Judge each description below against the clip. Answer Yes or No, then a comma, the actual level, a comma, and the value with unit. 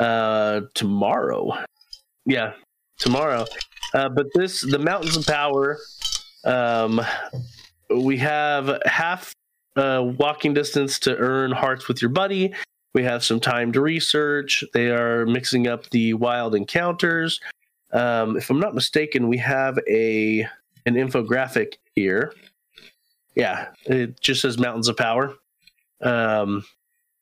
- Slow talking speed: Yes, slow, 125 wpm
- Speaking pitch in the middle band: No, low, 130 Hz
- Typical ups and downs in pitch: Yes, average, 3.7 semitones